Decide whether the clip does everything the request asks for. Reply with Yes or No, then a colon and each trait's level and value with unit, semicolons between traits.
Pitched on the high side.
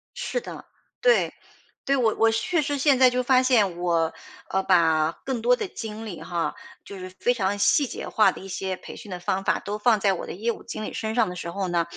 Yes: high, 210 Hz